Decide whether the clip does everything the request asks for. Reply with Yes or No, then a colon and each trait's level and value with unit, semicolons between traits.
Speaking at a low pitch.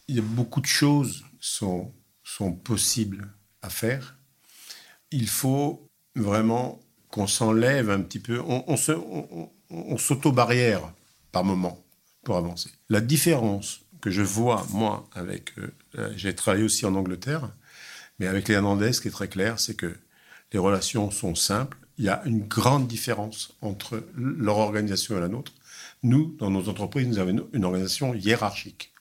Yes: low, 110 Hz